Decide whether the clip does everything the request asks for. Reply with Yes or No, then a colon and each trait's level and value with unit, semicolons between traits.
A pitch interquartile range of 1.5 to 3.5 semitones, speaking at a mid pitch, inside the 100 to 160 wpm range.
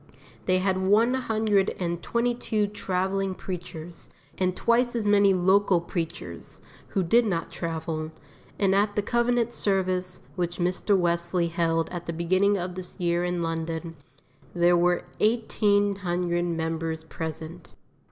Yes: average, 3.0 semitones; medium, 180 Hz; average, 140 wpm